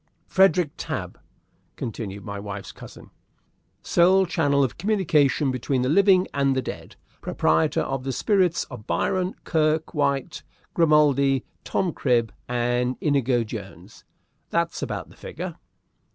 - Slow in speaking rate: Yes, slow, 125 wpm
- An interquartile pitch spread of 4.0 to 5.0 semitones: No, wide, 5.4 semitones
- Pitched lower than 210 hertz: Yes, medium, 140 Hz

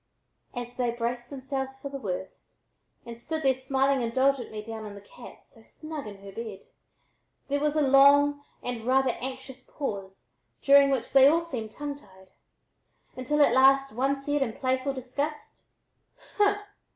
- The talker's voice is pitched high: Yes, very high, 265 Hz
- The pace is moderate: Yes, average, 160 wpm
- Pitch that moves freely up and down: No, average, 3.2 semitones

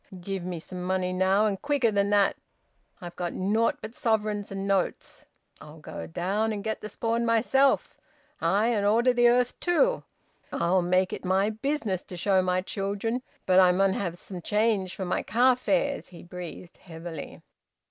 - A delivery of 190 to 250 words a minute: No, average, 175 wpm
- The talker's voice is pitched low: No, high, 200 Hz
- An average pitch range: Yes, average, 3.6 semitones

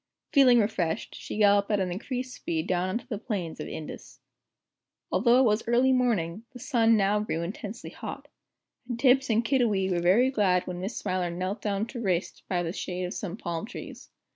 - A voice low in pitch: No, high, 205 Hz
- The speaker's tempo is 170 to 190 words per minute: No, average, 200 wpm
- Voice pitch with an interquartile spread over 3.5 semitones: Yes, average, 4.7 semitones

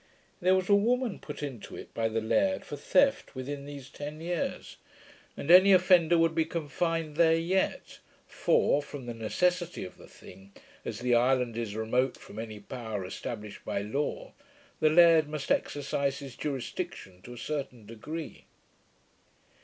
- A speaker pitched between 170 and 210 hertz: No, medium, 145 Hz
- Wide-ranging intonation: Yes, wide, 6.1 semitones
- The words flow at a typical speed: Yes, average, 160 wpm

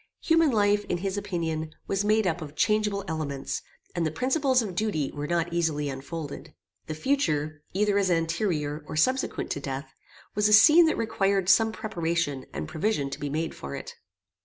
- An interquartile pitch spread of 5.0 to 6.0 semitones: Yes, wide, 5.6 semitones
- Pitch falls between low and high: Yes, medium, 170 Hz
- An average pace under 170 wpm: No, average, 180 wpm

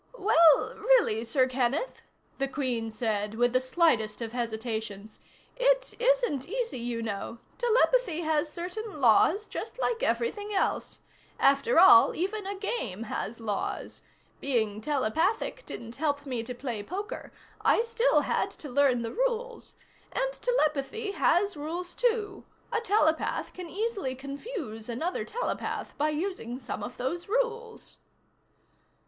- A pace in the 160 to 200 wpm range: No, slow, 135 wpm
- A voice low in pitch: No, very high, 310 Hz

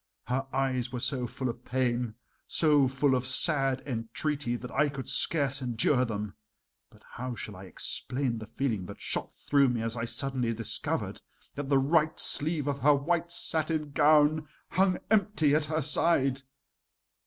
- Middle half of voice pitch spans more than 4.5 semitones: No, average, 3.5 semitones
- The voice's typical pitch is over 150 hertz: No, low, 135 Hz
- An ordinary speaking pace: Yes, average, 165 wpm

